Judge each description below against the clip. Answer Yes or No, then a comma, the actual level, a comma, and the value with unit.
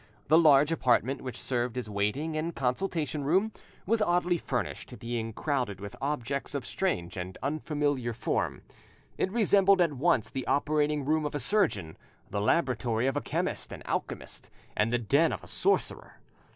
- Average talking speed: Yes, average, 165 wpm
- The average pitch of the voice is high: No, medium, 140 Hz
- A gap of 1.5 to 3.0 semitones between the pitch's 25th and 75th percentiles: No, average, 5.1 semitones